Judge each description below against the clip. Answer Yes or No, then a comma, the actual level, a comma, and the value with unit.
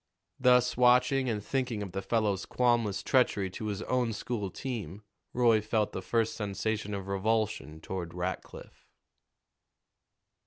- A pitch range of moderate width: Yes, average, 3.9 semitones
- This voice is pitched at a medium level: No, low, 110 Hz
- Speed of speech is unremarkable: No, slow, 130 wpm